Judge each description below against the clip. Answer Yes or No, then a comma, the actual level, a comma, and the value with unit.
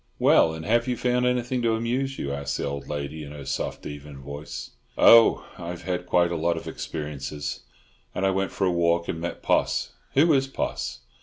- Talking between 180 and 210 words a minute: Yes, fast, 205 wpm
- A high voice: No, very low, 85 Hz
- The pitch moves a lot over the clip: Yes, wide, 7.9 semitones